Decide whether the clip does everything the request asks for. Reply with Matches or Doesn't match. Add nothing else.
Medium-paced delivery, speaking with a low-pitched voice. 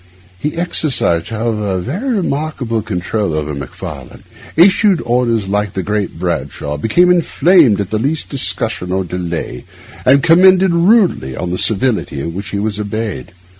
Matches